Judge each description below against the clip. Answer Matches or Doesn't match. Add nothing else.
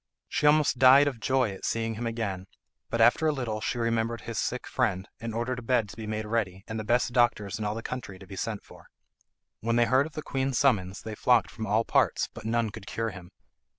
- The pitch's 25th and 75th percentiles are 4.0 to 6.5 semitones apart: Doesn't match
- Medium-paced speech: Doesn't match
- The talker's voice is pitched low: Matches